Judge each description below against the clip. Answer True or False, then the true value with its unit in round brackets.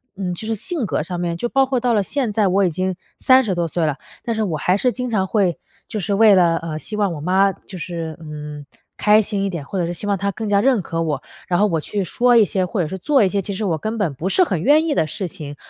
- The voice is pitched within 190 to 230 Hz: True (195 Hz)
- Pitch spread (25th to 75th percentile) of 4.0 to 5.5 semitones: True (4.3 semitones)